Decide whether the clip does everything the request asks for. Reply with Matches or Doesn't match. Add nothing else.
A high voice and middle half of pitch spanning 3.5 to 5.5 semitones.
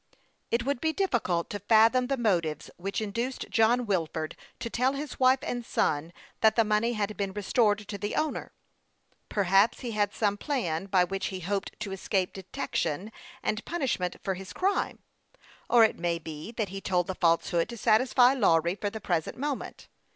Matches